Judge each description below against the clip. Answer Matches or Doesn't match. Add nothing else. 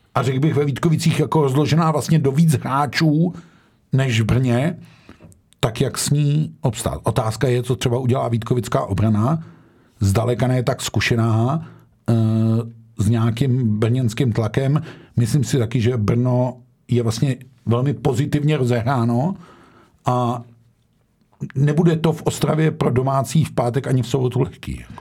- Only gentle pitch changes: Doesn't match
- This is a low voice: Matches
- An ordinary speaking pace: Matches